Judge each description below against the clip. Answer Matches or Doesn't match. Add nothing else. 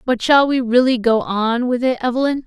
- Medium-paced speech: Doesn't match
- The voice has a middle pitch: Doesn't match